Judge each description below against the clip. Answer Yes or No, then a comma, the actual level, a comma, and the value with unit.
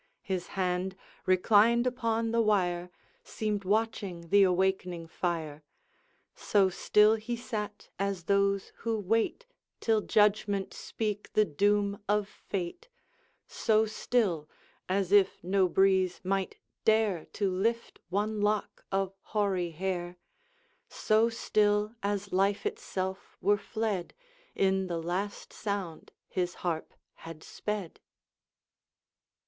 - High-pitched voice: Yes, high, 200 Hz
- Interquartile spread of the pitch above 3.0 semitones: No, narrow, 2.5 semitones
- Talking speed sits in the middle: No, slow, 115 wpm